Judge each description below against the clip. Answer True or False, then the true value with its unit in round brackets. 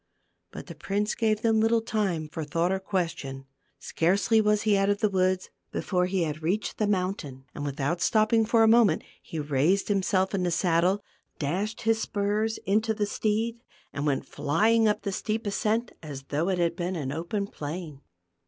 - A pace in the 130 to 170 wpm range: False (190 wpm)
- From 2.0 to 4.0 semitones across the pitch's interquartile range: False (4.5 semitones)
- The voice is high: True (195 Hz)